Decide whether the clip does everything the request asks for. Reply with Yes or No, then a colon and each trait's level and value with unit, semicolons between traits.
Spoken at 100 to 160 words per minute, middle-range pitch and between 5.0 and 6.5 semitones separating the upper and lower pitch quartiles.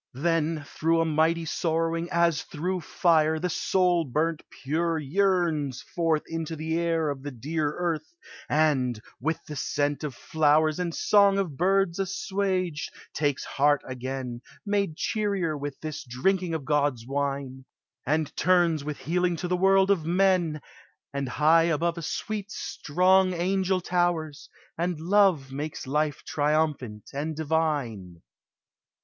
No: average, 140 wpm; medium, 160 Hz; average, 3.4 semitones